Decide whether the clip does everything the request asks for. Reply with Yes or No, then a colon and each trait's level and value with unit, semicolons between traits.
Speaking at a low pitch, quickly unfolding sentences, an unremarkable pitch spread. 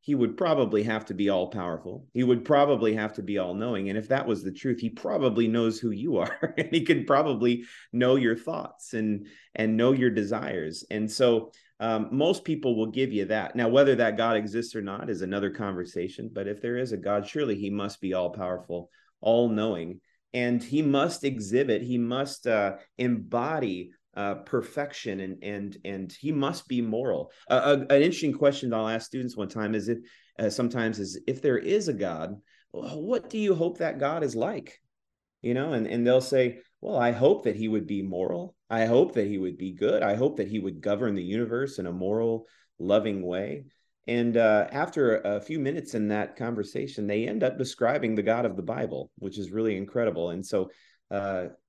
Yes: low, 115 Hz; fast, 210 wpm; average, 3.6 semitones